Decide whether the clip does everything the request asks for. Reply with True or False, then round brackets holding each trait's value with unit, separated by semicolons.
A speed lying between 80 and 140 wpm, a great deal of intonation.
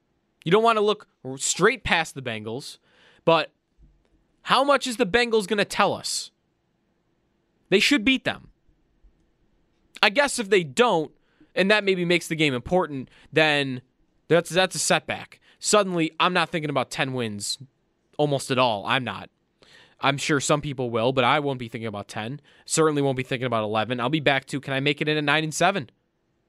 False (190 wpm; 6.0 semitones)